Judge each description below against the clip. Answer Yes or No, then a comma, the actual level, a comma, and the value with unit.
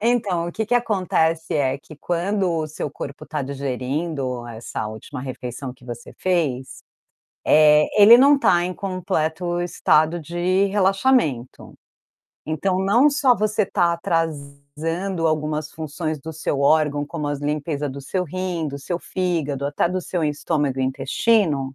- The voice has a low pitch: No, medium, 160 Hz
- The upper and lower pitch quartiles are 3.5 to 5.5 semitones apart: Yes, average, 4.5 semitones